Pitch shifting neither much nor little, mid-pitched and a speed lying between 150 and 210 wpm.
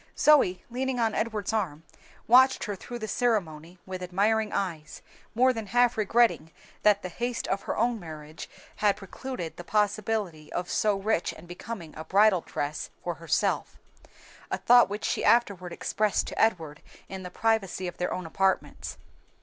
No: average, 4.2 semitones; high, 200 Hz; average, 165 wpm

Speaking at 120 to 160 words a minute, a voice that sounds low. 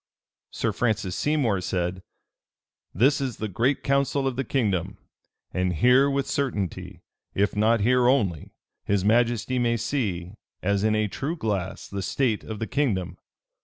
Yes: average, 150 wpm; low, 110 Hz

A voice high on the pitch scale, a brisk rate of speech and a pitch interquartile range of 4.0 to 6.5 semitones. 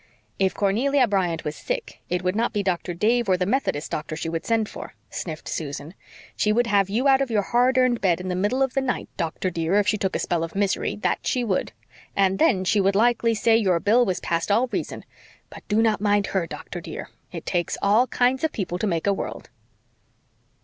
Yes: high, 200 Hz; fast, 225 wpm; average, 4.6 semitones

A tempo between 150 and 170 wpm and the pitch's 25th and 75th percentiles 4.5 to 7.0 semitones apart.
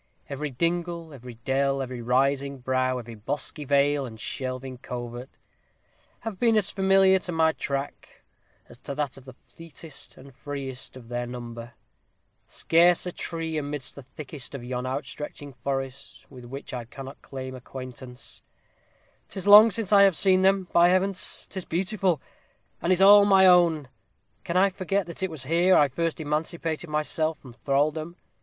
Yes: average, 165 wpm; average, 5.1 semitones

